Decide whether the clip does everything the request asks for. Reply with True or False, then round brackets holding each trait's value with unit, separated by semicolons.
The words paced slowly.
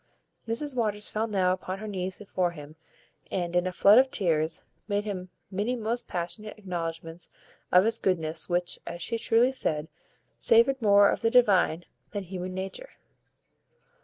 False (160 wpm)